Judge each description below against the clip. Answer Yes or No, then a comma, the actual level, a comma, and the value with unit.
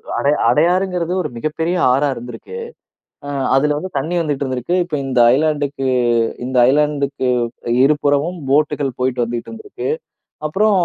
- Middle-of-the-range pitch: Yes, medium, 145 Hz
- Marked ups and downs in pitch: No, average, 3.7 semitones